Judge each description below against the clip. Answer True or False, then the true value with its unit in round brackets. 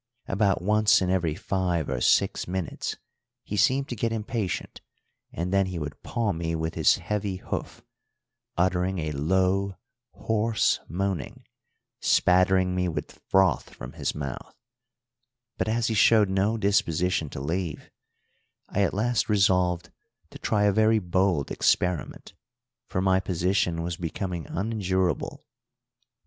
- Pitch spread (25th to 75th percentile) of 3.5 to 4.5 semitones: False (2.9 semitones)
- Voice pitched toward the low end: True (95 Hz)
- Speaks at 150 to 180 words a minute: False (135 wpm)